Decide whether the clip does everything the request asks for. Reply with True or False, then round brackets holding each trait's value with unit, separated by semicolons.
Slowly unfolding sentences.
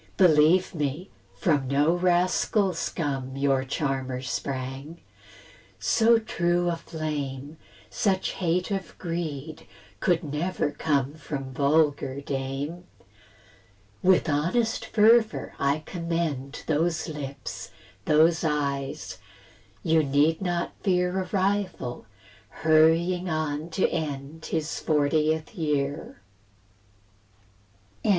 True (100 wpm)